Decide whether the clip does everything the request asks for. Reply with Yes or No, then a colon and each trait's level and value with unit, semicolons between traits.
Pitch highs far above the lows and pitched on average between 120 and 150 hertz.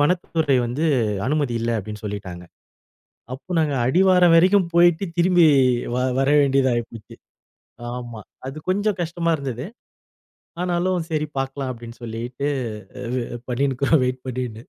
Yes: wide, 5.8 semitones; medium, 140 Hz